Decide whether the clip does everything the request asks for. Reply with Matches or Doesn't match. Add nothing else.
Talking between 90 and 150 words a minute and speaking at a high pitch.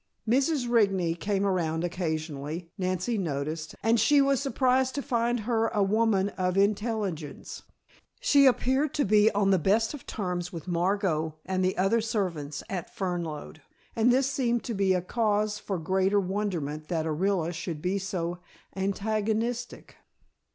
Matches